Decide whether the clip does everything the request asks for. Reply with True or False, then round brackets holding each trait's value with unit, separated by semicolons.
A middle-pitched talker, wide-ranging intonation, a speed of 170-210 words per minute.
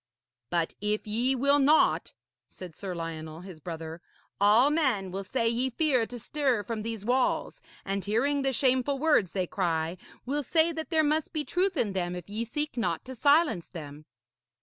False (230 Hz; 7.5 semitones; 180 wpm)